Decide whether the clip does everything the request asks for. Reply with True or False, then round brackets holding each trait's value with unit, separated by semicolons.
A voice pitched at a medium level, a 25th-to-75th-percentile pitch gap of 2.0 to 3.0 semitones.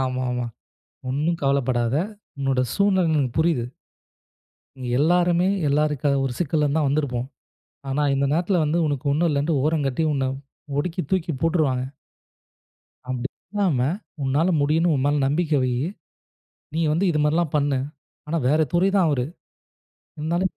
False (150 Hz; 3.8 semitones)